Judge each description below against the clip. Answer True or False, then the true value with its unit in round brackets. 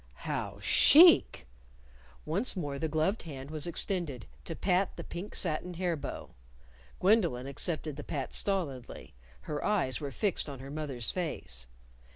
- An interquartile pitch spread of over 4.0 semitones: True (4.8 semitones)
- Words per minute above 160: False (145 wpm)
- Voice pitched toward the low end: False (155 Hz)